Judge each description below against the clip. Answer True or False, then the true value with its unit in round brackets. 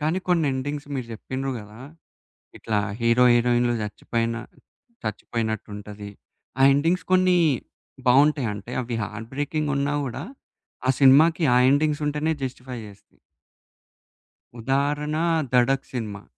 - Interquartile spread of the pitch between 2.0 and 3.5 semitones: False (4.2 semitones)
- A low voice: True (130 Hz)